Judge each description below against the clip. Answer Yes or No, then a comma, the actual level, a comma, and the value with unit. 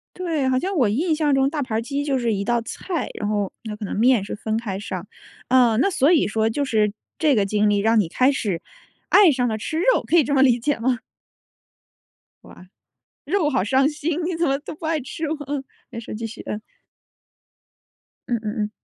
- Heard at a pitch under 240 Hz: No, very high, 255 Hz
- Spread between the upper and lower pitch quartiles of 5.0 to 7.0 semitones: Yes, wide, 5.5 semitones